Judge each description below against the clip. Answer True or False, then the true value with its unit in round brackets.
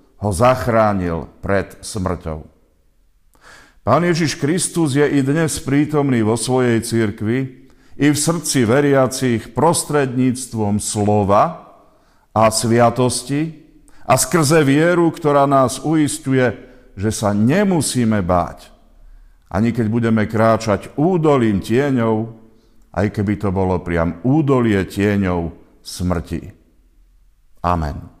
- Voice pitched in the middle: False (115 Hz)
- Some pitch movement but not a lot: False (6.1 semitones)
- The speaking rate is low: True (100 wpm)